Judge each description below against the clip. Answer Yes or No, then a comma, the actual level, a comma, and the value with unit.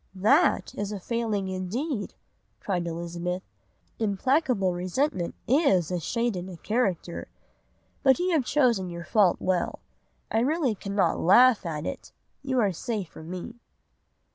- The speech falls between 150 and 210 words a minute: No, average, 140 wpm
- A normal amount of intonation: No, wide, 5.7 semitones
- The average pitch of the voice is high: Yes, high, 200 Hz